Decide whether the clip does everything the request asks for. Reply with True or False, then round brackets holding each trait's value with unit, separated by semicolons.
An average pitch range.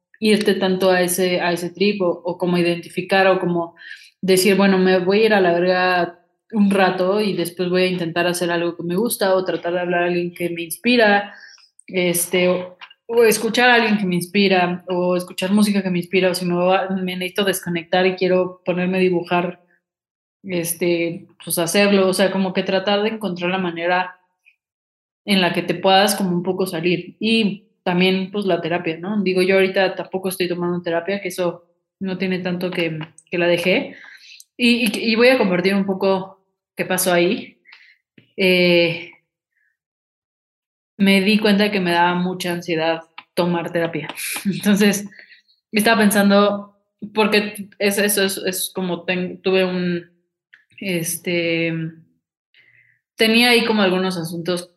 False (2.0 semitones)